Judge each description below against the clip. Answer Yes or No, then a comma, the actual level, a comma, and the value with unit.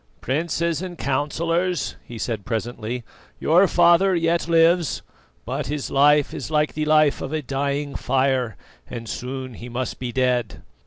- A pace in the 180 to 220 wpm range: No, average, 150 wpm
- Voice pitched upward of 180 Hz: No, medium, 140 Hz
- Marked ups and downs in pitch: No, average, 4.7 semitones